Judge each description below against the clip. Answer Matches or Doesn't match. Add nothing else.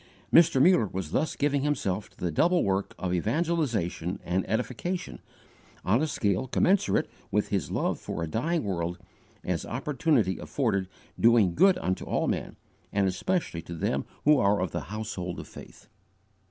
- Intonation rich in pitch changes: Matches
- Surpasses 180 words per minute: Doesn't match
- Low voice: Matches